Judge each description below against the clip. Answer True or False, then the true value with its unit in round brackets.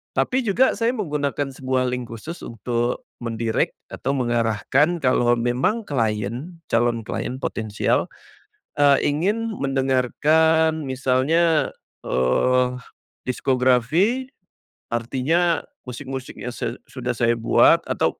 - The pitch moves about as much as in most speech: True (5.0 semitones)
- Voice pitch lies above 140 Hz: False (130 Hz)